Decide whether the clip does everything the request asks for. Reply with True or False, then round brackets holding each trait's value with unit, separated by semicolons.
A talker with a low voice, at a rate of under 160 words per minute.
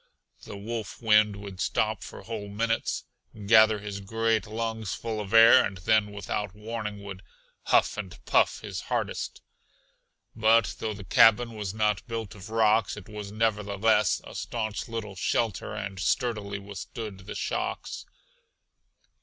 True (105 Hz; 145 wpm)